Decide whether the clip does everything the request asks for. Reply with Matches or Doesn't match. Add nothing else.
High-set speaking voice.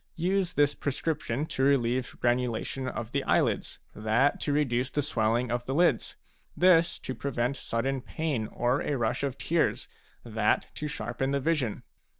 Doesn't match